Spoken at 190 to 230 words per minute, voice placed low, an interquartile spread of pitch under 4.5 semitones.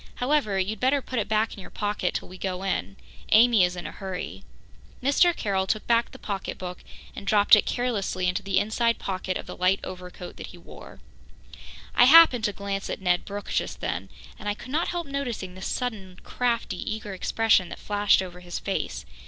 No: average, 200 wpm; high, 205 Hz; average, 3.9 semitones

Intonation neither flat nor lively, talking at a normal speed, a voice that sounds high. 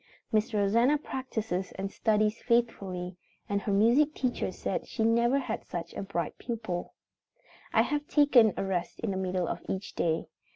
Yes: average, 3.9 semitones; average, 170 wpm; high, 215 Hz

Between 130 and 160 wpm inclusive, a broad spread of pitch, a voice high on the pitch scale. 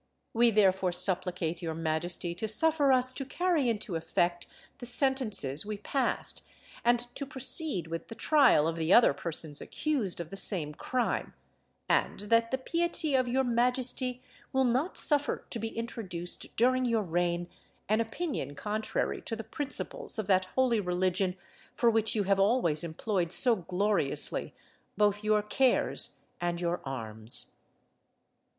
Yes: average, 150 wpm; wide, 6.3 semitones; high, 215 Hz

